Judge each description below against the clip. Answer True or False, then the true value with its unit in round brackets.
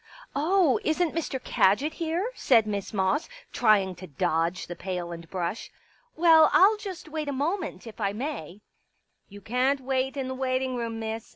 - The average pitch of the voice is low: False (255 Hz)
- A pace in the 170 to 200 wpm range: True (190 wpm)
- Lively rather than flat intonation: True (7.9 semitones)